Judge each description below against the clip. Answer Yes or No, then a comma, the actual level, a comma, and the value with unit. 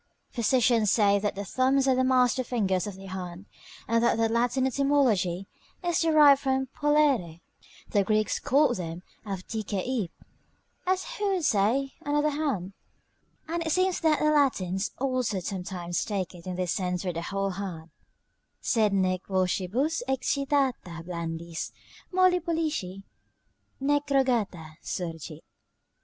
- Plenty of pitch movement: Yes, wide, 7.0 semitones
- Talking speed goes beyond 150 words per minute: No, slow, 135 wpm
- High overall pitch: Yes, high, 225 Hz